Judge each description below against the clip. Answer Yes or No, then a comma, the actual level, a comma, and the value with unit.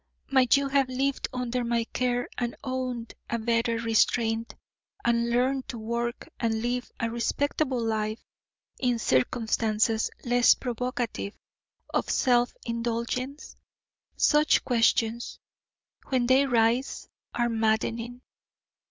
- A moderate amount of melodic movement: No, narrow, 1.7 semitones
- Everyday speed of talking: No, slow, 110 wpm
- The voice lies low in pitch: No, high, 240 Hz